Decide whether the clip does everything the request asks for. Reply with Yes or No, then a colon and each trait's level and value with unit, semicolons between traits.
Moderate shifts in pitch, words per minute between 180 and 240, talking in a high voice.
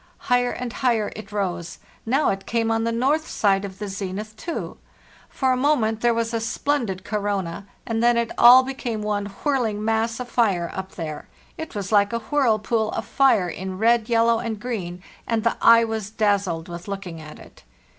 Yes: average, 3.2 semitones; average, 190 wpm; high, 220 Hz